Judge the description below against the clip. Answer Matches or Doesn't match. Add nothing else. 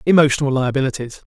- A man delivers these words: Matches